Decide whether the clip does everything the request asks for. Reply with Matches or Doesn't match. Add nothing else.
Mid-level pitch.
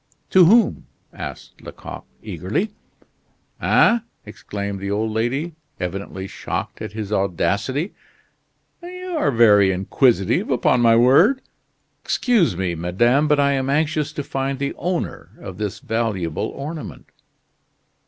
Doesn't match